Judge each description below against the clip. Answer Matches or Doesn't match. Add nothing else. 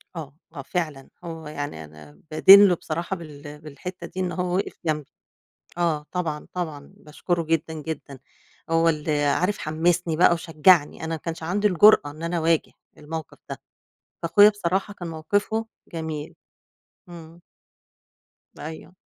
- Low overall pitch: Doesn't match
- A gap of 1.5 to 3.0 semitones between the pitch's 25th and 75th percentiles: Matches